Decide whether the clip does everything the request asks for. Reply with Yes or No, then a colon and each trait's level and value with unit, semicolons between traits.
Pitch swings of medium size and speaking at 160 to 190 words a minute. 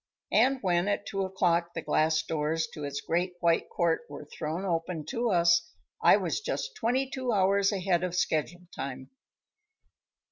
Yes: average, 3.4 semitones; average, 165 wpm